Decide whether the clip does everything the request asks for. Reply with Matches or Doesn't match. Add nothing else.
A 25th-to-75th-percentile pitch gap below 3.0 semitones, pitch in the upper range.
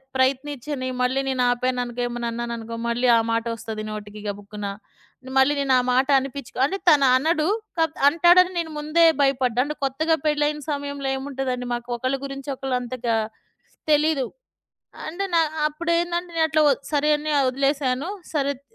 Doesn't match